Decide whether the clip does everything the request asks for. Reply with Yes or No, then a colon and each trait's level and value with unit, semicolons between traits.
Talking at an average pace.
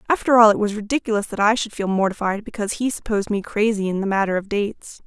No: fast, 235 wpm